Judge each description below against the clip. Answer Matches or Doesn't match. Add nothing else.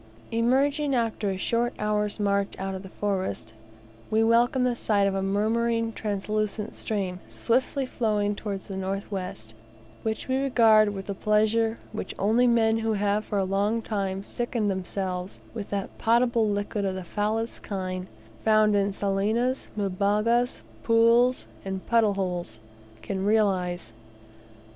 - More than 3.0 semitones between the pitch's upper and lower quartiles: Doesn't match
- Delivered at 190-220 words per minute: Doesn't match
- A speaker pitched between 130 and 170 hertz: Doesn't match